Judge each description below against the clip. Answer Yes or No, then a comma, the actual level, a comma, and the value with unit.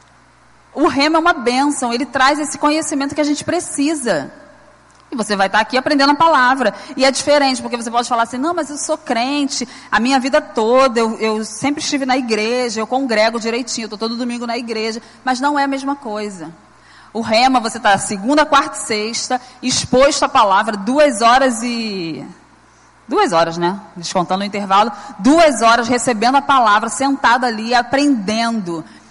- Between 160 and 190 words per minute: Yes, average, 180 wpm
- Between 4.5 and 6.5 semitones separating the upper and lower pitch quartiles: No, average, 4.0 semitones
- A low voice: No, very high, 250 Hz